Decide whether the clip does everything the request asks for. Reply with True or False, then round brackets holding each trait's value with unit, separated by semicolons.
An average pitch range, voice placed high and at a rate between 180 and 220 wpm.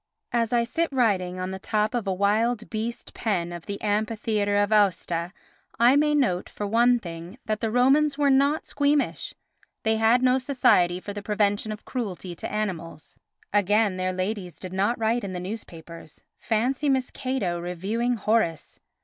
False (4.6 semitones; 215 Hz; 170 wpm)